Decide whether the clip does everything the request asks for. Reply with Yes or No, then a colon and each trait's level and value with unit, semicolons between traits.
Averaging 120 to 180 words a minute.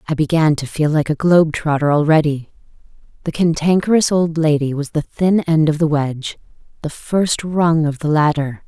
Yes: average, 175 wpm